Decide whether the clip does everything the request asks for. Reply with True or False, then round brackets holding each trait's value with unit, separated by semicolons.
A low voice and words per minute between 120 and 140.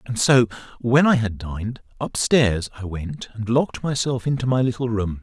False (120 Hz; 195 wpm)